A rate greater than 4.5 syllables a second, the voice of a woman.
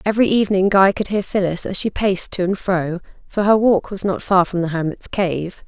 Yes: 5.5 syllables/s; female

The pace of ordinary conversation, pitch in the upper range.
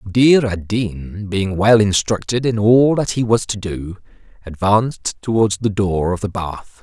No: average, 175 wpm; low, 105 Hz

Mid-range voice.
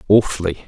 No: very low, 95 Hz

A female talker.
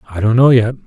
No: male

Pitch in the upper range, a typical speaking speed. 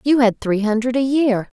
No: high, 240 Hz; fast, 225 wpm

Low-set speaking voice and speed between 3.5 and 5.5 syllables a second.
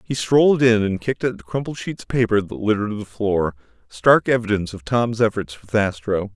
No: low, 110 Hz; 5.7 syllables/s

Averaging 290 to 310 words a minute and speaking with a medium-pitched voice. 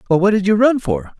Yes: fast, 300 wpm; medium, 180 Hz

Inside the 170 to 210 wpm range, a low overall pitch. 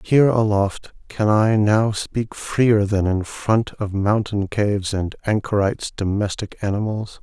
No: average, 140 wpm; low, 105 Hz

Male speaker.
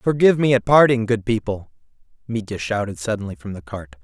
Yes: male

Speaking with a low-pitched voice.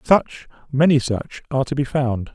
Yes: low, 130 Hz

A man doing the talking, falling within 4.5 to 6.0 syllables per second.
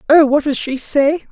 No: female; 4.6 syllables/s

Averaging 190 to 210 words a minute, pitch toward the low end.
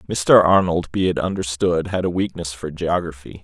No: average, 175 wpm; very low, 90 Hz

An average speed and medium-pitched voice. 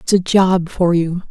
No: fast, 230 wpm; medium, 180 Hz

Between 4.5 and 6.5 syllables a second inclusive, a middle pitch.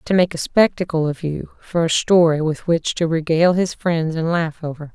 Yes: 5.0 syllables/s; medium, 165 Hz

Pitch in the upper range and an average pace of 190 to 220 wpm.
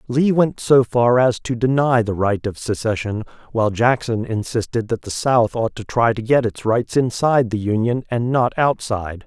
No: low, 120 Hz; average, 195 wpm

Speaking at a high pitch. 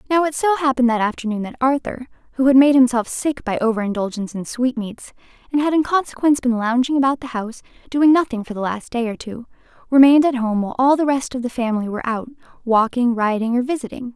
Yes: very high, 250 Hz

